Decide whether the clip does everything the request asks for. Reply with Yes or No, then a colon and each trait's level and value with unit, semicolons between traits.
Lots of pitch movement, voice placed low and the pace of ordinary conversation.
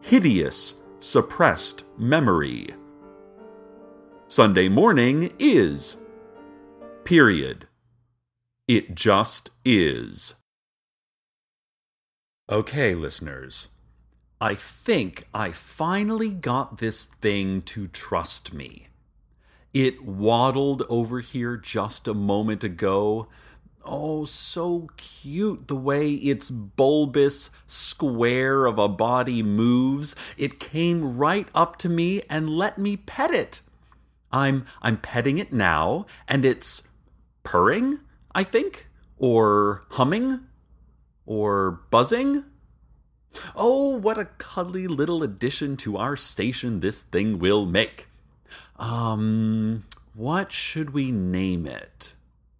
No: wide, 7.5 semitones; low, 125 Hz; slow, 100 wpm